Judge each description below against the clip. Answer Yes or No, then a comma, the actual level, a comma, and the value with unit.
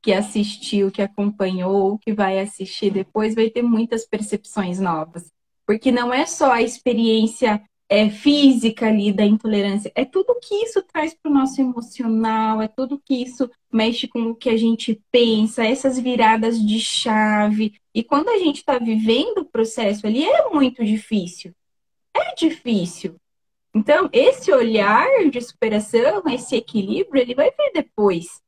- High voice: Yes, high, 225 Hz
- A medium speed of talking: Yes, average, 155 wpm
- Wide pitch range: No, average, 4.0 semitones